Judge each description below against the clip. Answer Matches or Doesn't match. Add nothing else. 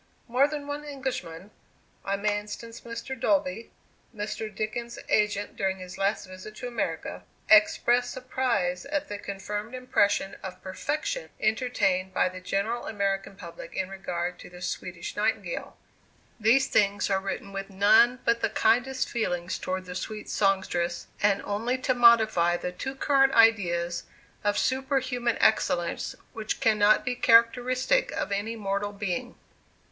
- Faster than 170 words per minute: Doesn't match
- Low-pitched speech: Doesn't match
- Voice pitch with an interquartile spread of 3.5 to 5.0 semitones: Matches